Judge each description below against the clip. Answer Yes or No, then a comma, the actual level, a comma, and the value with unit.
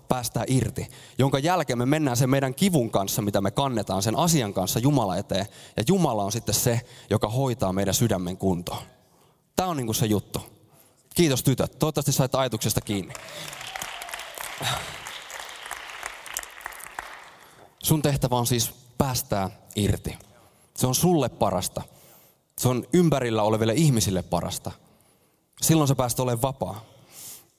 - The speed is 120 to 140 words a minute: Yes, average, 130 wpm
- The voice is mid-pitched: No, low, 125 Hz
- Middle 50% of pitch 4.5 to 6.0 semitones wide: Yes, average, 4.9 semitones